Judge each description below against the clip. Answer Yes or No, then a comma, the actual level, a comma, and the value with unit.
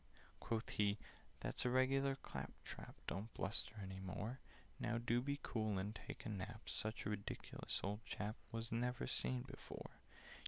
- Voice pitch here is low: Yes, low, 110 Hz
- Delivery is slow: No, average, 155 wpm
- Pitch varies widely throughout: No, average, 3.0 semitones